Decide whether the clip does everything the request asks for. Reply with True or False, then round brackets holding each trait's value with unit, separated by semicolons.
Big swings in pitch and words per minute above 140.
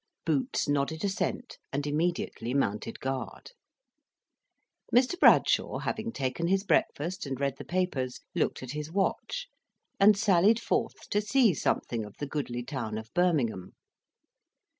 False (7.2 semitones; 135 wpm)